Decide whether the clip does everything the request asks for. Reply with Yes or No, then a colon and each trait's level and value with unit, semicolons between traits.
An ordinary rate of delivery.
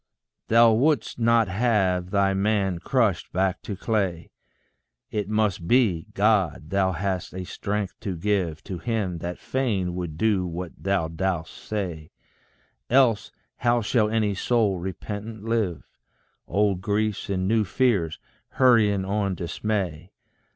No: slow, 130 wpm